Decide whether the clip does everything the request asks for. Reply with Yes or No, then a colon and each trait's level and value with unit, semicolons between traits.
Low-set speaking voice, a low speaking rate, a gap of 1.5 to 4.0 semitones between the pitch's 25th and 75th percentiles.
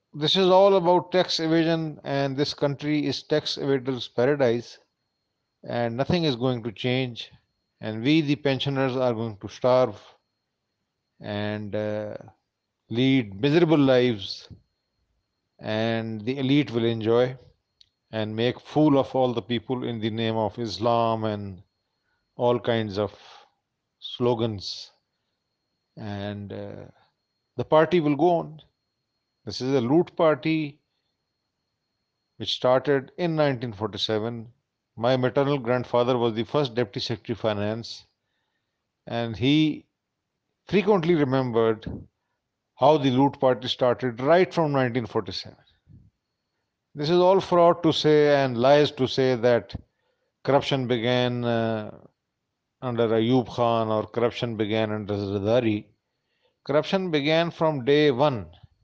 No: low, 125 Hz; slow, 120 wpm; average, 4.5 semitones